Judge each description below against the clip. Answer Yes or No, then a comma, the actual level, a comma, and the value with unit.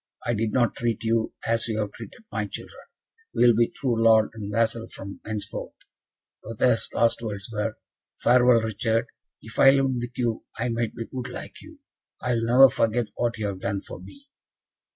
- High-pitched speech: No, low, 115 Hz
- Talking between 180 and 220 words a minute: Yes, average, 190 wpm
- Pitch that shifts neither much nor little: No, narrow, 1.7 semitones